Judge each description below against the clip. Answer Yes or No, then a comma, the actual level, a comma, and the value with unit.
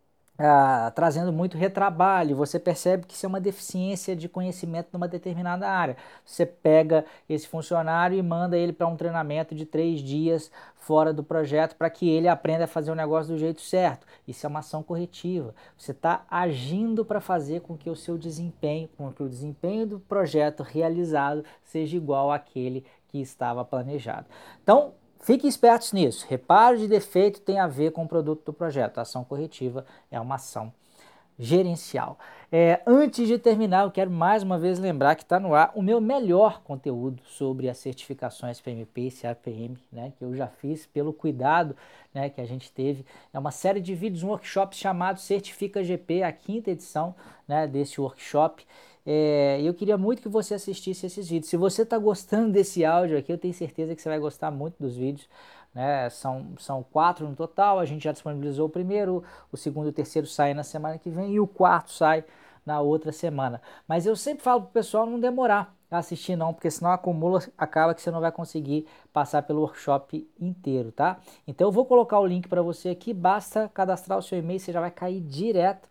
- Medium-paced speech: No, fast, 195 wpm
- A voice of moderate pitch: Yes, medium, 165 Hz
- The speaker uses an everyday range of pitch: Yes, average, 3.9 semitones